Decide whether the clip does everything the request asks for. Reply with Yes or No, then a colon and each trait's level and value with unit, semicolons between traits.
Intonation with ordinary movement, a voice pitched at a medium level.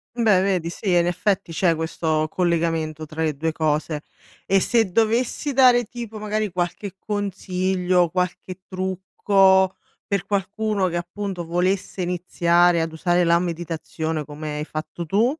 Yes: average, 3.1 semitones; medium, 180 Hz